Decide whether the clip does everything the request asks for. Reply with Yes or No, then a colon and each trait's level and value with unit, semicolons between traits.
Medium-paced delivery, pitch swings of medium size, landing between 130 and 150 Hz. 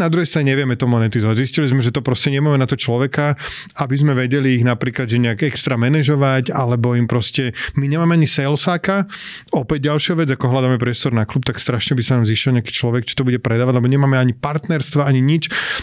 No: fast, 215 wpm; average, 3.1 semitones; low, 135 Hz